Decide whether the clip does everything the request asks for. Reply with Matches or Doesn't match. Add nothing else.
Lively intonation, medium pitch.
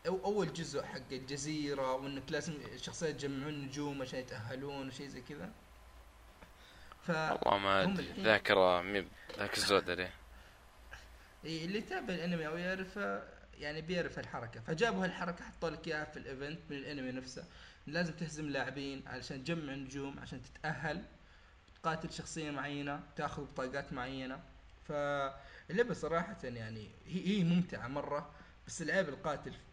Doesn't match